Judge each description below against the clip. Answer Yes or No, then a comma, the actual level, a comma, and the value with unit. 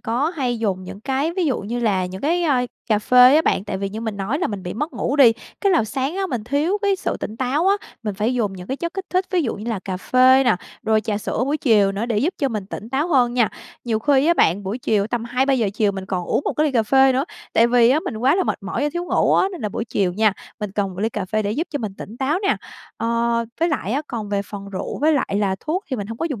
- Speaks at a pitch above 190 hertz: Yes, high, 235 Hz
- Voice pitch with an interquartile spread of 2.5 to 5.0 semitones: No, wide, 5.4 semitones